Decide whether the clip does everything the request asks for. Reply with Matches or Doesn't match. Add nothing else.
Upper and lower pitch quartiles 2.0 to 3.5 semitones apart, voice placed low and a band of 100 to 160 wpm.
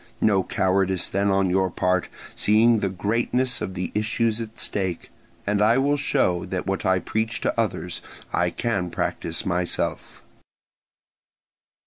Matches